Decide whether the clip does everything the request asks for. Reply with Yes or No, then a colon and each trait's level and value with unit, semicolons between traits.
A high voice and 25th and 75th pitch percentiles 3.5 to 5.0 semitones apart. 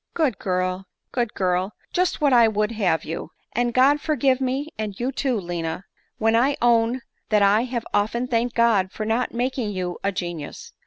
Yes: high, 225 Hz; average, 4.7 semitones